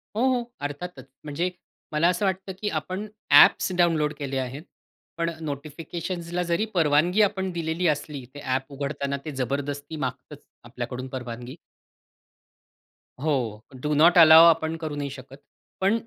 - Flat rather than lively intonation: No, average, 3.8 semitones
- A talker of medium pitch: Yes, medium, 150 Hz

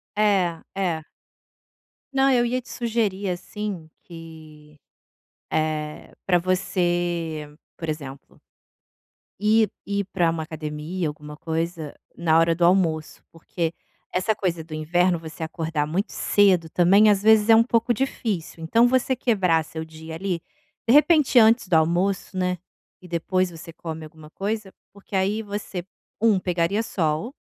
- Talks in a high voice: No, medium, 175 Hz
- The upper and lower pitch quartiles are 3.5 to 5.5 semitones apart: Yes, average, 4.3 semitones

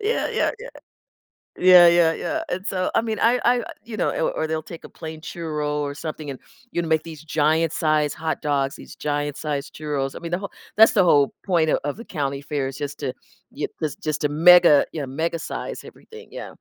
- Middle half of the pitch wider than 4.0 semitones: No, average, 3.3 semitones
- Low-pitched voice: No, medium, 160 Hz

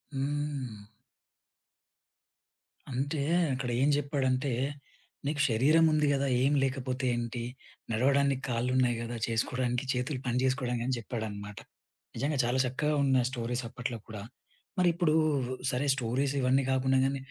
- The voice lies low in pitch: Yes, low, 130 Hz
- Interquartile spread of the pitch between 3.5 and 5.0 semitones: No, narrow, 2.5 semitones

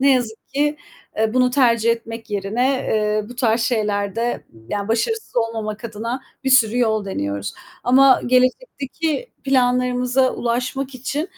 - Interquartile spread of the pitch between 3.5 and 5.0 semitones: No, average, 3.0 semitones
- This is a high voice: Yes, high, 245 Hz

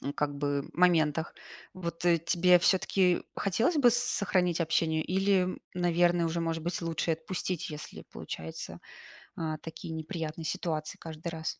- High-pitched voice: No, medium, 170 Hz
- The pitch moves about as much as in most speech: No, narrow, 2.2 semitones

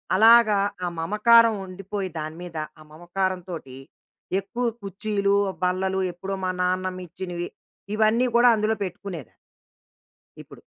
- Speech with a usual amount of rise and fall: Yes, average, 3.0 semitones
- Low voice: No, high, 190 Hz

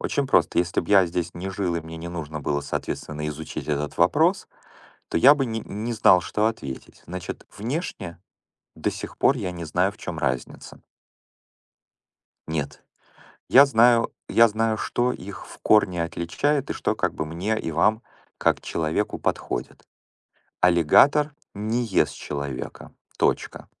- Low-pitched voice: Yes, very low, 90 Hz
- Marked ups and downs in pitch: Yes, wide, 5.7 semitones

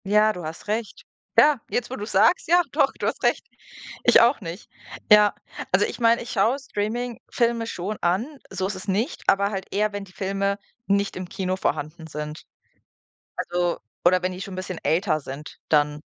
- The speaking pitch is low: No, high, 200 Hz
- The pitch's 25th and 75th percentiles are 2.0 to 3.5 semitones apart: No, average, 4.1 semitones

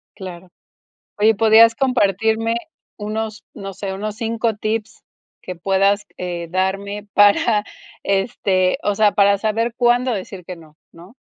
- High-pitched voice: Yes, high, 205 Hz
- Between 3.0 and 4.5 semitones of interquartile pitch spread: No, narrow, 2.5 semitones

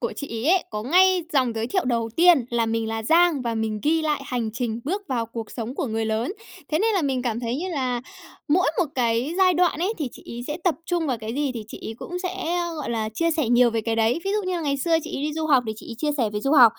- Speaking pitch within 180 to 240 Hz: No, very high, 265 Hz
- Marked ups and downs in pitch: Yes, wide, 6.4 semitones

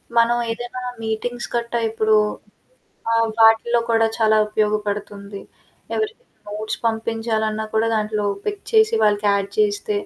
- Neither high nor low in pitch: No, high, 225 Hz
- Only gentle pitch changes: Yes, narrow, 1.9 semitones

